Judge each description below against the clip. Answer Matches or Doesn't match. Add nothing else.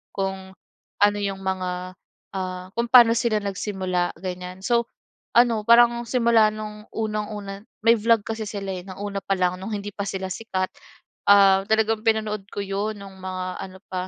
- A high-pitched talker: Matches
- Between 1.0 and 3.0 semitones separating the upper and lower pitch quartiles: Matches